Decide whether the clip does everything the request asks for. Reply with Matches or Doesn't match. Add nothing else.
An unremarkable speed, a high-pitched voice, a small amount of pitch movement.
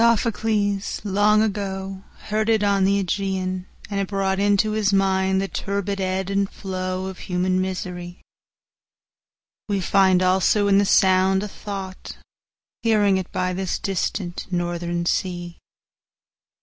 Doesn't match